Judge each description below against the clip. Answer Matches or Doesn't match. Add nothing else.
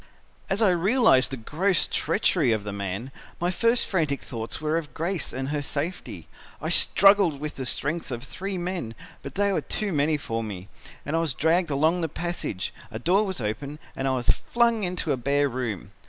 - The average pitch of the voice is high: Doesn't match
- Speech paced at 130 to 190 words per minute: Doesn't match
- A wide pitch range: Matches